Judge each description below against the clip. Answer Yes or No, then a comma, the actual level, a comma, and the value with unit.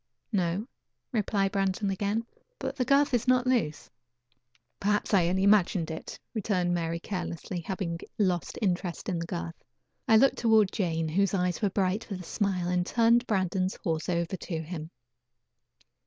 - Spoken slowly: No, average, 155 wpm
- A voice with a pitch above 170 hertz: Yes, high, 190 Hz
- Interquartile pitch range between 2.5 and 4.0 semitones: Yes, average, 3.5 semitones